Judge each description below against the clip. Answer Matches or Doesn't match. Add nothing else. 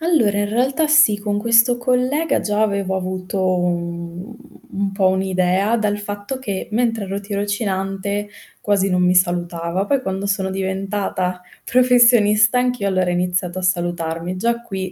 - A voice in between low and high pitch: Doesn't match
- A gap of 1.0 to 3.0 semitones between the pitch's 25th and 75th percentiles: Doesn't match